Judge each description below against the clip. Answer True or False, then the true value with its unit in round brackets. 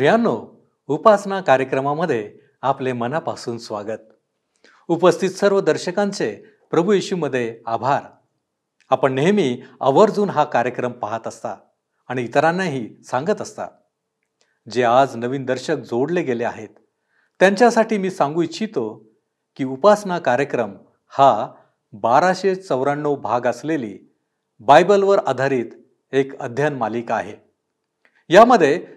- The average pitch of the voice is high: False (145 Hz)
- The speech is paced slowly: False (95 wpm)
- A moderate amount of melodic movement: False (6.5 semitones)